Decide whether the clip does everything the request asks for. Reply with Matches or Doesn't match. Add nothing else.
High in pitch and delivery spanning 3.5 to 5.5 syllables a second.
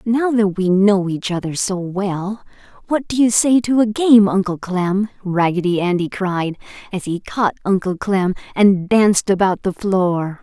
Matches